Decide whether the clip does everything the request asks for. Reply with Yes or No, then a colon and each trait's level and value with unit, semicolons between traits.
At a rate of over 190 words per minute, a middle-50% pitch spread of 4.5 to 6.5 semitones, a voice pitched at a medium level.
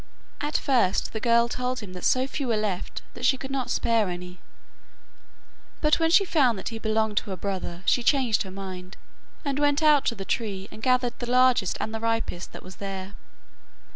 No: average, 200 wpm; average, 4.9 semitones; high, 230 Hz